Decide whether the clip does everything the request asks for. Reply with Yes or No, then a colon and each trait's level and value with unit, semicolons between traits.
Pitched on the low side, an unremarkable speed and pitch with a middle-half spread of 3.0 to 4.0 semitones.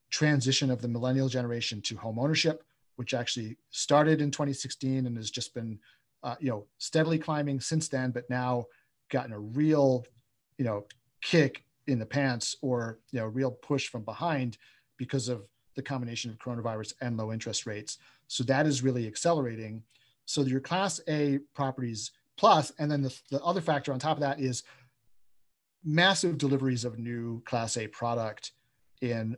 Yes: low, 130 Hz; average, 165 wpm; average, 3.3 semitones